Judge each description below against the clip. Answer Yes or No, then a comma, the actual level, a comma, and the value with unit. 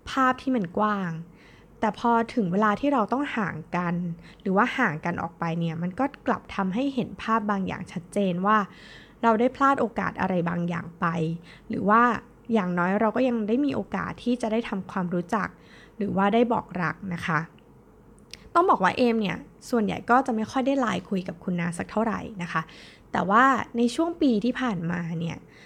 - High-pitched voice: Yes, high, 210 Hz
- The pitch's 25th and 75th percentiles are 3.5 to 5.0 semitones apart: No, wide, 5.4 semitones